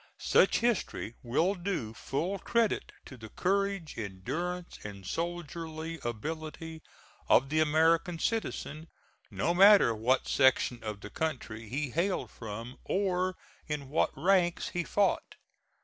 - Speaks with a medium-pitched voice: Yes, medium, 160 Hz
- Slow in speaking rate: Yes, slow, 125 wpm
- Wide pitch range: Yes, wide, 6.3 semitones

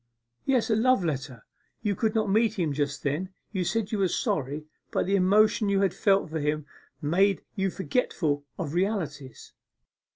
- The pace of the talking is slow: No, average, 170 wpm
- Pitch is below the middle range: No, high, 190 Hz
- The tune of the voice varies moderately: No, wide, 5.9 semitones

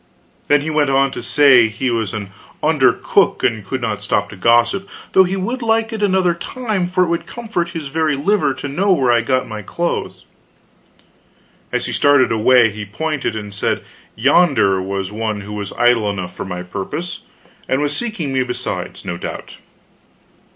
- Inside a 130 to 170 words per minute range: No, average, 185 wpm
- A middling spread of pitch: No, wide, 8.2 semitones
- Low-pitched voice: Yes, low, 130 Hz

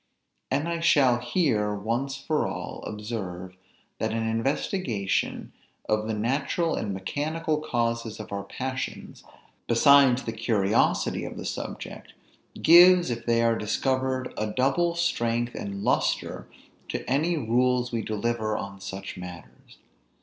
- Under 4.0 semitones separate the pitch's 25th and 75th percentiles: No, average, 4.4 semitones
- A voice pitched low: Yes, low, 120 Hz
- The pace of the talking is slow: Yes, slow, 130 wpm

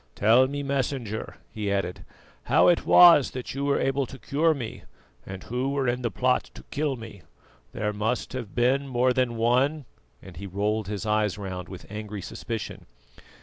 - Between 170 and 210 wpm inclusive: Yes, average, 180 wpm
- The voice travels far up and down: No, average, 4.3 semitones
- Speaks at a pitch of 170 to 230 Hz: No, low, 120 Hz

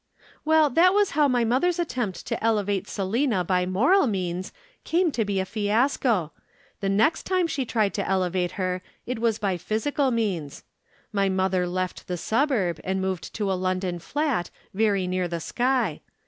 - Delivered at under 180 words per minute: Yes, average, 165 wpm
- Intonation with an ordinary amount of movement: No, wide, 5.7 semitones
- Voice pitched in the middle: No, high, 205 Hz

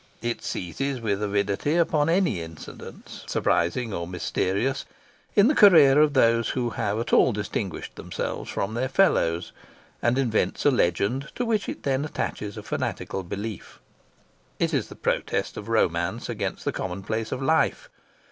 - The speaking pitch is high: No, low, 115 Hz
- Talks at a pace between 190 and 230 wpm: No, average, 155 wpm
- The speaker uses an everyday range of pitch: No, wide, 6.0 semitones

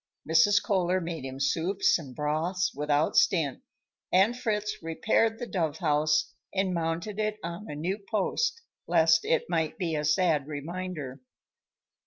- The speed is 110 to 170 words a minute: Yes, average, 145 wpm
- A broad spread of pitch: No, average, 4.2 semitones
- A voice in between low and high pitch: Yes, medium, 170 Hz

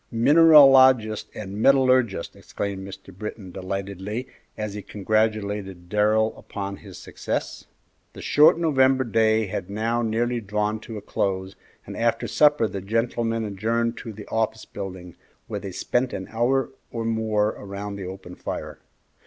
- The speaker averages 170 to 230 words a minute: No, average, 145 wpm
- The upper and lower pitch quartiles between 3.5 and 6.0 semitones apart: No, average, 2.9 semitones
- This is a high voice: No, low, 110 Hz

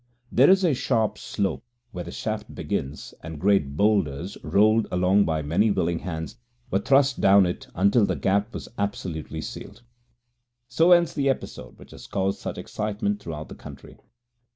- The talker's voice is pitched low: Yes, low, 100 Hz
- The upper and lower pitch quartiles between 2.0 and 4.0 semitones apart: No, average, 4.8 semitones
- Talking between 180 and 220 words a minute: No, average, 165 wpm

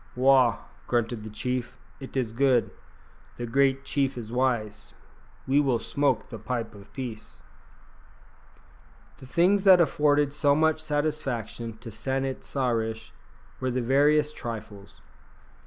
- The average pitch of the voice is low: Yes, low, 130 Hz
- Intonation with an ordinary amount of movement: Yes, average, 3.7 semitones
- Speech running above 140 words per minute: No, slow, 135 wpm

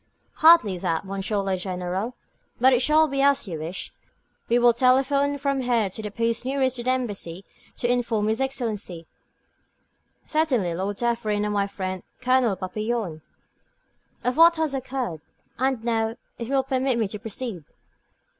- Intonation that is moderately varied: Yes, average, 4.9 semitones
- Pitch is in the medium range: No, high, 235 Hz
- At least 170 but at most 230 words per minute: No, average, 160 wpm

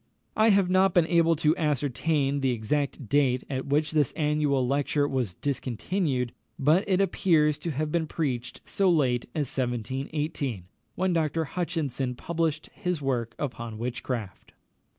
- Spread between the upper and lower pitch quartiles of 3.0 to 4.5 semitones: Yes, average, 4.2 semitones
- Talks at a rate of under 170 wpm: Yes, average, 145 wpm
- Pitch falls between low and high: Yes, medium, 145 Hz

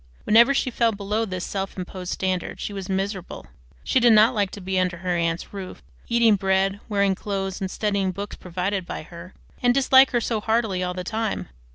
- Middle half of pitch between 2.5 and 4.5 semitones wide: Yes, average, 3.1 semitones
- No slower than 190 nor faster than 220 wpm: Yes, average, 200 wpm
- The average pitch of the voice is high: Yes, high, 195 Hz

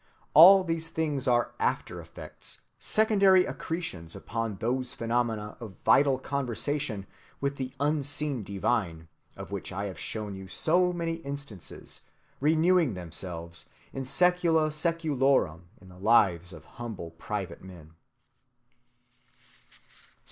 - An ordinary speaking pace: No, slow, 110 wpm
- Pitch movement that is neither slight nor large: No, wide, 8.3 semitones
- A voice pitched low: Yes, low, 125 Hz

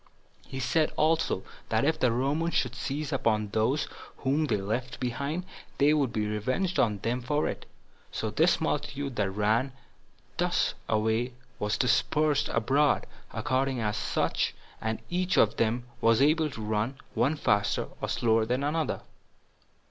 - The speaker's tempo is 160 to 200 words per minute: No, average, 145 wpm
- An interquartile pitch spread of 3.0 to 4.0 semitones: No, average, 5.0 semitones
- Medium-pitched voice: No, low, 130 Hz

